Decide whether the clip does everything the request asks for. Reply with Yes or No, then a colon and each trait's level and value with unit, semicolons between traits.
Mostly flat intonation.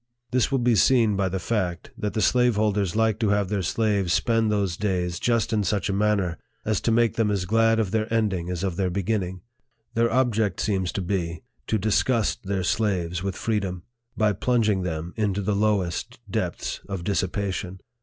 No: average, 3.2 semitones